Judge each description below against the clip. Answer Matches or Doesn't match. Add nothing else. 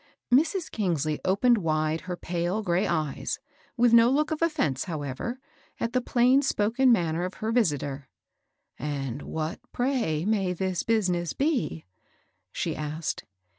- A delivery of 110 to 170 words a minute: Matches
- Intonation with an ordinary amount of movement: Doesn't match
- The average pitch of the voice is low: Doesn't match